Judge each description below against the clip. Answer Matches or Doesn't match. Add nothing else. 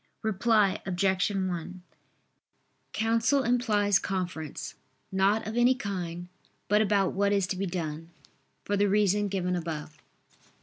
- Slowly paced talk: Matches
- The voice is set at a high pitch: Matches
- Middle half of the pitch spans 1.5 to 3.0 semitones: Matches